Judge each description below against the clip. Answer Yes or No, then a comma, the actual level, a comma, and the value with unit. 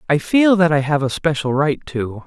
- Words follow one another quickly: Yes, fast, 240 wpm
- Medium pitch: Yes, medium, 155 Hz